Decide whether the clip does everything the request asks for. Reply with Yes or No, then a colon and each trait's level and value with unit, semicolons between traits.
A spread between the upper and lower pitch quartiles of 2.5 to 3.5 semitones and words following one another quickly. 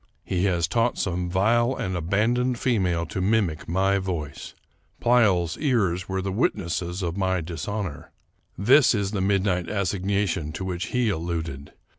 No: average, 3.2 semitones; average, 150 wpm